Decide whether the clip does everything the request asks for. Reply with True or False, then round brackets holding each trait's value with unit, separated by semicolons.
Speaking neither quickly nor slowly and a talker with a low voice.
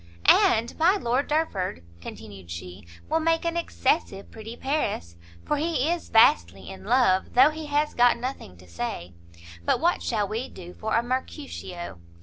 False (160 wpm; 235 Hz)